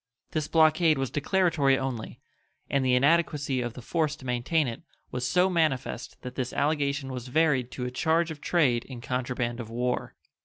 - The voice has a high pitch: No, low, 135 Hz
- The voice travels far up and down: No, average, 4.0 semitones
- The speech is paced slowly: No, average, 180 wpm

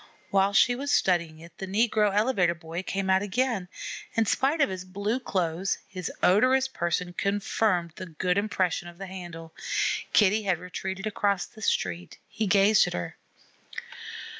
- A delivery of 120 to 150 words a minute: No, average, 160 wpm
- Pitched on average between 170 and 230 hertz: Yes, high, 190 Hz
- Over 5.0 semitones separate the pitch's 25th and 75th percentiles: No, average, 3.2 semitones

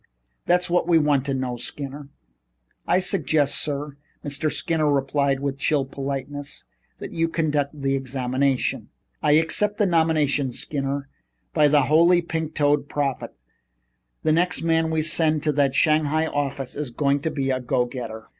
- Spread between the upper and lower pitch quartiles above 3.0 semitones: No, narrow, 2.5 semitones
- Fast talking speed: No, average, 160 wpm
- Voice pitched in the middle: Yes, medium, 145 Hz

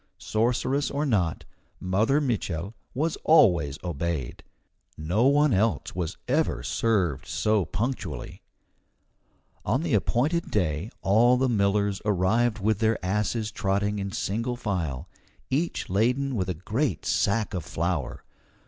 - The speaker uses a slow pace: Yes, slow, 125 wpm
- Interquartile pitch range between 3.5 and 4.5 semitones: No, average, 5.0 semitones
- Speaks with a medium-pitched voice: No, low, 105 Hz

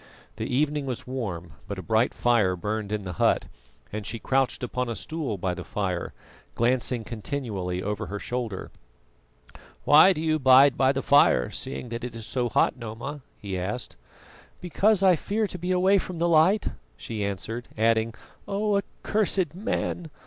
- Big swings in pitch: Yes, wide, 6.8 semitones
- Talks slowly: No, average, 170 wpm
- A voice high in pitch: No, low, 125 Hz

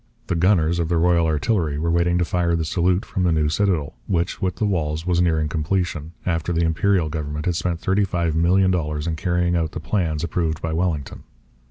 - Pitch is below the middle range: Yes, very low, 85 Hz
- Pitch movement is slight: Yes, narrow, 2.1 semitones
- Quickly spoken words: Yes, fast, 210 wpm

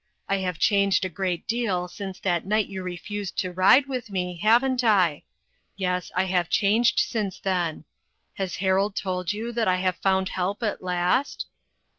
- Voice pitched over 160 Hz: Yes, high, 190 Hz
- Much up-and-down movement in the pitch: No, narrow, 2.5 semitones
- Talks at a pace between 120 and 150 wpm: No, average, 170 wpm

